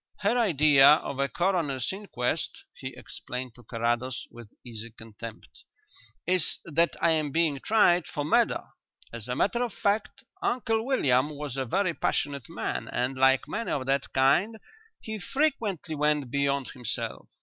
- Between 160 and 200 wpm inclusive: No, average, 150 wpm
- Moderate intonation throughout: No, wide, 6.7 semitones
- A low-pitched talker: No, medium, 145 Hz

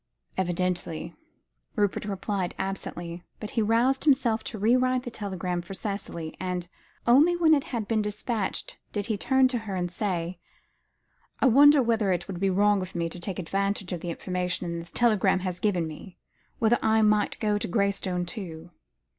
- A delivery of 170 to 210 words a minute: Yes, average, 175 wpm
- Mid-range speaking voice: No, high, 200 Hz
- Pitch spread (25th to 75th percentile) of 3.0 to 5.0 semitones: Yes, average, 3.8 semitones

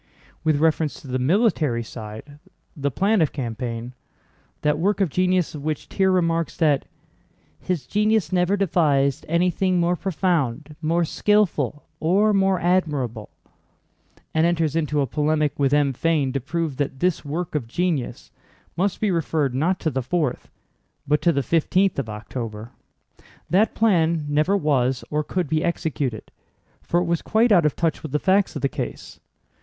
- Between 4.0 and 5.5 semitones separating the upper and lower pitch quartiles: Yes, average, 4.5 semitones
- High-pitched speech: No, medium, 155 Hz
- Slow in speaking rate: No, average, 155 wpm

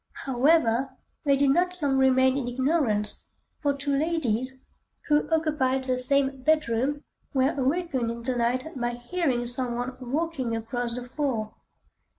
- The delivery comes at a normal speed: Yes, average, 145 wpm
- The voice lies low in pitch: No, very high, 260 Hz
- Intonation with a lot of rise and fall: No, average, 3.0 semitones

